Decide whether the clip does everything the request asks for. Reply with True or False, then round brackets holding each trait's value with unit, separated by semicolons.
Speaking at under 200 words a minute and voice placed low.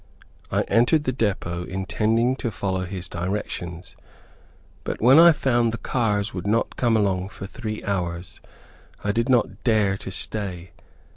True (150 wpm; 105 Hz)